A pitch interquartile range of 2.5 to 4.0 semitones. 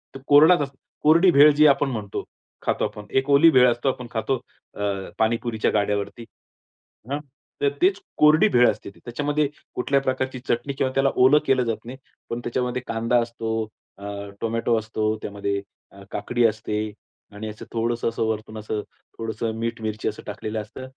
Yes: average, 3.7 semitones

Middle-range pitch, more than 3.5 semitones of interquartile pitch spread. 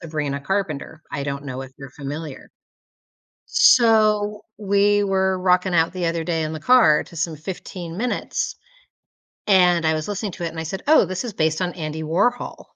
Yes: medium, 170 Hz; average, 4.2 semitones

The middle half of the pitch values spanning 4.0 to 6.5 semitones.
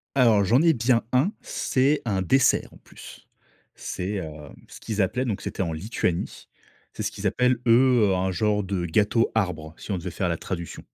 Yes: average, 5.3 semitones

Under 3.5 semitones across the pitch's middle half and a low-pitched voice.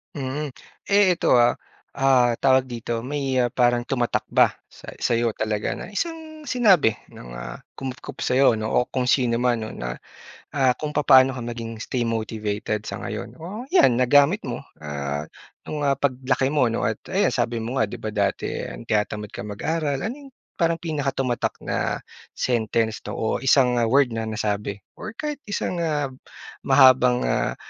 No: average, 4.2 semitones; low, 125 Hz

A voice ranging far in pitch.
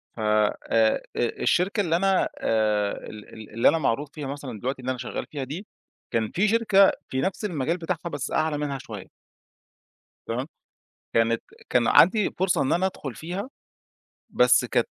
Yes: wide, 7.6 semitones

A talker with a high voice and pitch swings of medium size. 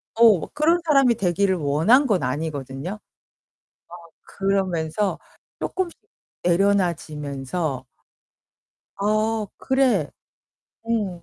No: high, 195 Hz; wide, 6.0 semitones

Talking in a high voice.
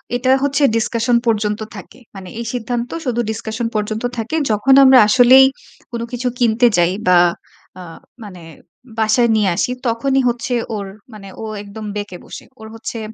Yes: high, 225 Hz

